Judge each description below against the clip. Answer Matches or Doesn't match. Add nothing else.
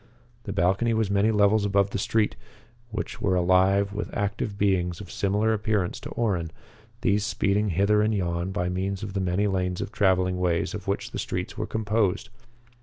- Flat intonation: Matches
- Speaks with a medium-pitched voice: Doesn't match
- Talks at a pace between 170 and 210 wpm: Matches